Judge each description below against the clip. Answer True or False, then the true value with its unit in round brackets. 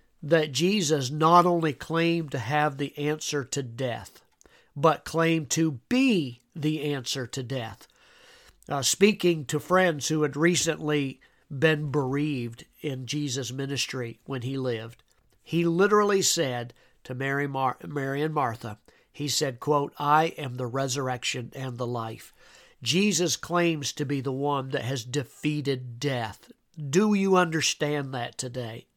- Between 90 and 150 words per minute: True (140 wpm)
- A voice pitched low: False (145 Hz)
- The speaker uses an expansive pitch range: False (3.5 semitones)